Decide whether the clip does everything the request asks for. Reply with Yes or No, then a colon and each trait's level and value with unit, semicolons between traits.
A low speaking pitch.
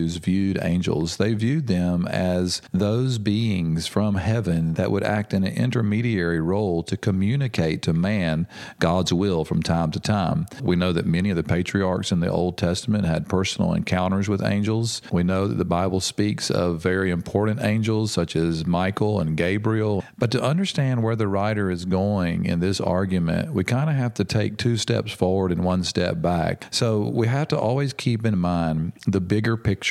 Yes: very low, 95 Hz